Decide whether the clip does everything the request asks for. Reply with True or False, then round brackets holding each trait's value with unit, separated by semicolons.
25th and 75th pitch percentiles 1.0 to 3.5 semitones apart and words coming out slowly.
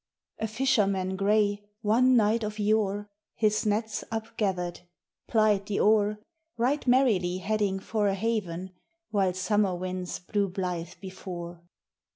True (2.7 semitones; 125 wpm)